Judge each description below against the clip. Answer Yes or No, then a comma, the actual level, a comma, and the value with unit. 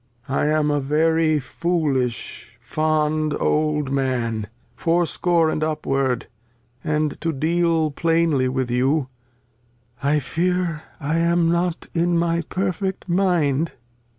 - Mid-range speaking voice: Yes, medium, 155 Hz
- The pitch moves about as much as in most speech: Yes, average, 3.4 semitones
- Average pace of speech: No, slow, 115 wpm